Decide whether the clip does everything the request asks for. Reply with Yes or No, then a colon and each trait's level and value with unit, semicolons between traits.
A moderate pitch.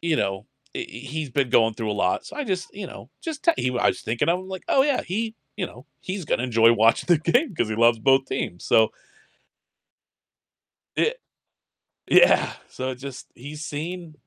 Yes: medium, 145 Hz